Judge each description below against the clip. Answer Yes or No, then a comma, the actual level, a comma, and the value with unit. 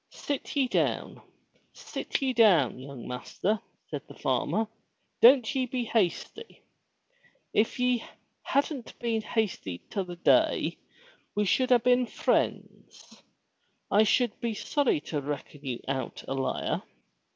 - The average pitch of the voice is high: Yes, high, 225 Hz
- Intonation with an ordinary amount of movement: No, wide, 8.4 semitones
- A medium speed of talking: No, slow, 130 wpm